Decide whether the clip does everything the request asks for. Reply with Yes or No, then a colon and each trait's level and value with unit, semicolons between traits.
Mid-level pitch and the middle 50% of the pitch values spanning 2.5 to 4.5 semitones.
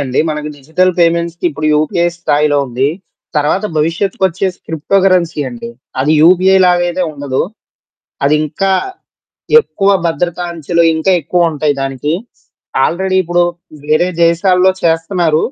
Yes: medium, 165 Hz; average, 3.2 semitones